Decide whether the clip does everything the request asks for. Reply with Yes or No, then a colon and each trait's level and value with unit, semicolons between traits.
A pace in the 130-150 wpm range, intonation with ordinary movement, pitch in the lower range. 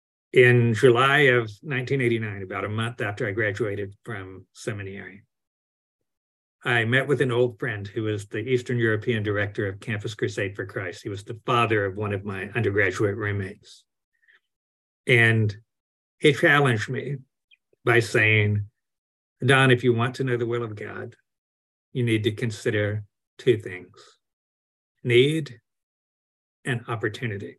Yes: average, 140 wpm; average, 3.5 semitones; low, 110 Hz